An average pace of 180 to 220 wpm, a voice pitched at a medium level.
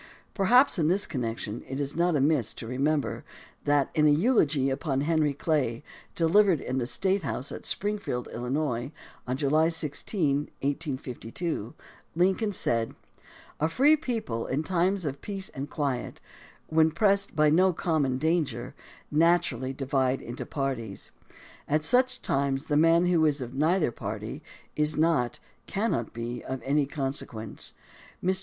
No: average, 150 wpm; medium, 150 Hz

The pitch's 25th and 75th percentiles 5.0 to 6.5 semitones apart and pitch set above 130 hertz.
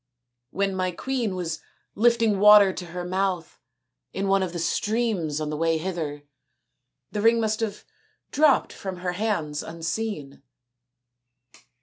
No: average, 4.5 semitones; medium, 185 Hz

